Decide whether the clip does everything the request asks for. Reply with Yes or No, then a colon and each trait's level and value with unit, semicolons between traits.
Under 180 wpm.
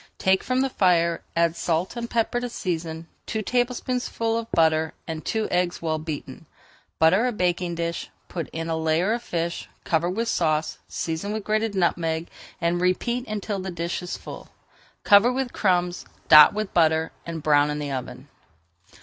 Yes: average, 170 wpm